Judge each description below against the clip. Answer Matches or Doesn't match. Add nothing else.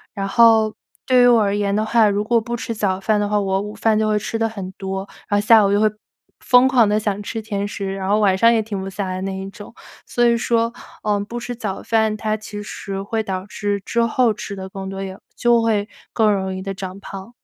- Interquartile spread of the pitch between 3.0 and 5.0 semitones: Doesn't match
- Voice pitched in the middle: Doesn't match